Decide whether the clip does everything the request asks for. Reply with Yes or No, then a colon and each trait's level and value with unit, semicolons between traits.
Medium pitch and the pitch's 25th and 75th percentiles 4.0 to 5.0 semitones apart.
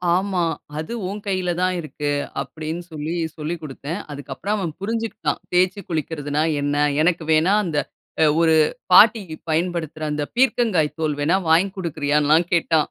No: medium, 165 Hz; average, 3.4 semitones